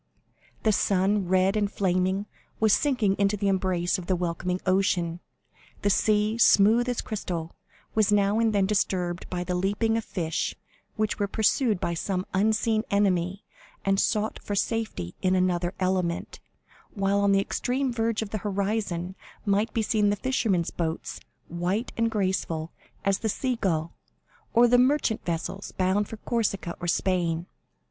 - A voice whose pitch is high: Yes, high, 195 Hz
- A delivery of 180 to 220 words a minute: No, average, 155 wpm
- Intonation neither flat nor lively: Yes, average, 3.0 semitones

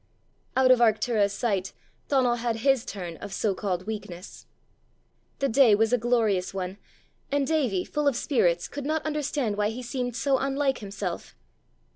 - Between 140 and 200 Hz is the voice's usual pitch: No, high, 230 Hz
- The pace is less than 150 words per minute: No, average, 160 wpm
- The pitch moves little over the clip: No, average, 5.0 semitones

